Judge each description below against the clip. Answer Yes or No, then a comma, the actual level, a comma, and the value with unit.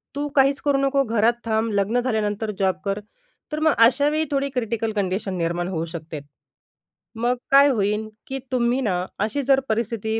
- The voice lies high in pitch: Yes, high, 225 Hz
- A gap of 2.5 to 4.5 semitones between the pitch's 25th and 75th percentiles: No, average, 5.0 semitones